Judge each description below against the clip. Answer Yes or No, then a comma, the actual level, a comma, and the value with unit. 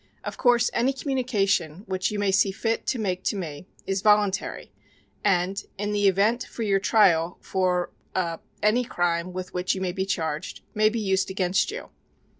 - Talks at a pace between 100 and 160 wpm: No, average, 180 wpm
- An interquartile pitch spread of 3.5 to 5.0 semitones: No, average, 2.8 semitones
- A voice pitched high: Yes, high, 195 Hz